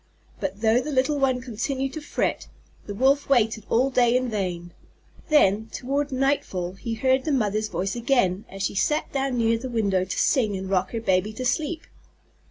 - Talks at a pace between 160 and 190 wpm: Yes, average, 185 wpm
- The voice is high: Yes, high, 235 Hz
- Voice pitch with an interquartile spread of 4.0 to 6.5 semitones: Yes, average, 5.1 semitones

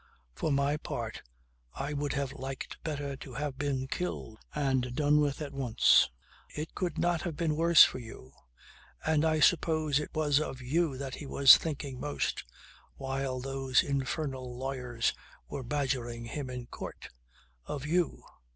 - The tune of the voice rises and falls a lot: No, narrow, 2.4 semitones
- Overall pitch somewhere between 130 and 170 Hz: Yes, medium, 140 Hz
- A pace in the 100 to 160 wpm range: Yes, average, 155 wpm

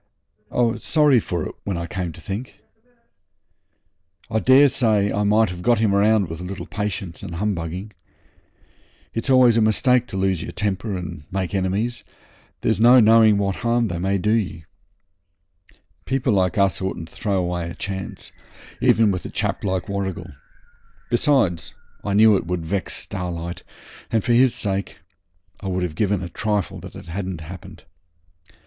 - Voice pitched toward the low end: Yes, low, 100 Hz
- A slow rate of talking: No, average, 165 wpm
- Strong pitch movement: No, average, 3.5 semitones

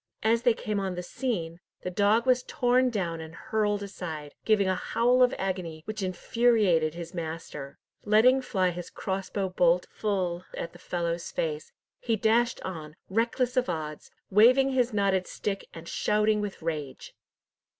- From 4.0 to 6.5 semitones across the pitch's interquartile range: Yes, average, 4.9 semitones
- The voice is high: Yes, high, 195 Hz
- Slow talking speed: No, average, 160 wpm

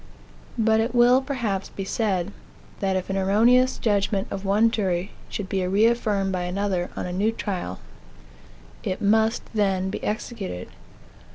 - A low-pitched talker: No, high, 200 Hz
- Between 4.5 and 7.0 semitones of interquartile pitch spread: No, average, 2.8 semitones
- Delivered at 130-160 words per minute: Yes, average, 150 wpm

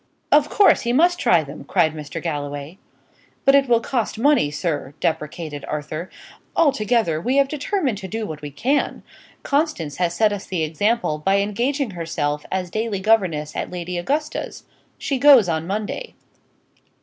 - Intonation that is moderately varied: No, wide, 8.7 semitones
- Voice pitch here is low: No, high, 195 Hz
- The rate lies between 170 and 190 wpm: No, average, 160 wpm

